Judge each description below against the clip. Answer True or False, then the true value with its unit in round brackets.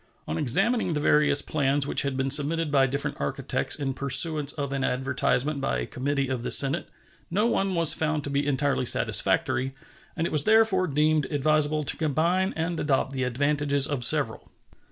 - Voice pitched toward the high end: False (145 Hz)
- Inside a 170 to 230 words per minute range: True (180 wpm)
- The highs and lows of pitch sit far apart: False (2.5 semitones)